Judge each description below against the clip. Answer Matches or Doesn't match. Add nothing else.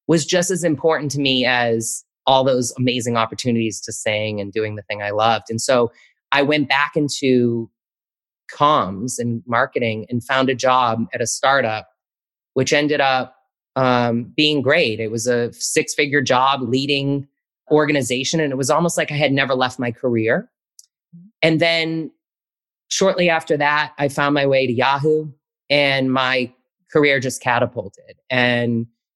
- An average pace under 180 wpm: Matches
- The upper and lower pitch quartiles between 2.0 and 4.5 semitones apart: Matches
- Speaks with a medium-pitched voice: Doesn't match